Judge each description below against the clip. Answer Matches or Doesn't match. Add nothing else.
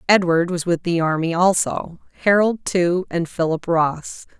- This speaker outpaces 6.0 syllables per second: Doesn't match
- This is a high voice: Doesn't match